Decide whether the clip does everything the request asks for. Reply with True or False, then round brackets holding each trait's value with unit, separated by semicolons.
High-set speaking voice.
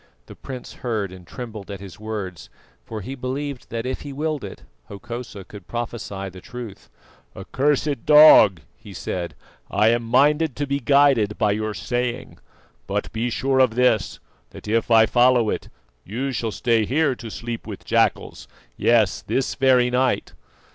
False (120 Hz)